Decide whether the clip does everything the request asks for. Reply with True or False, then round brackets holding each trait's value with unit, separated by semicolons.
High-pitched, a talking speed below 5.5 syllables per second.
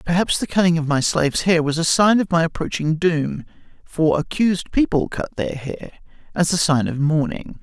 False (165 Hz; 5.3 syllables/s)